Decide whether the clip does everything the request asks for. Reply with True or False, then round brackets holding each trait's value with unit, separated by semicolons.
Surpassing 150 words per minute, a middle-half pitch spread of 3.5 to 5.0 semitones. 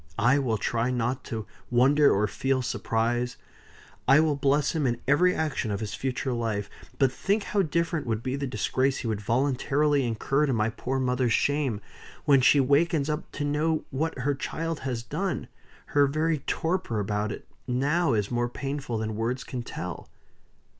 True (175 wpm; 3.9 semitones)